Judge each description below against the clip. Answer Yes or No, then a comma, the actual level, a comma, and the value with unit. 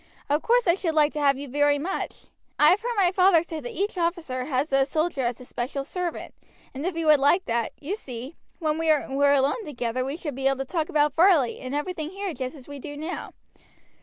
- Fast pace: Yes, fast, 235 wpm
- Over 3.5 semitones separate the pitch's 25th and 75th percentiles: Yes, average, 4.1 semitones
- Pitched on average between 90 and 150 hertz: No, very high, 295 Hz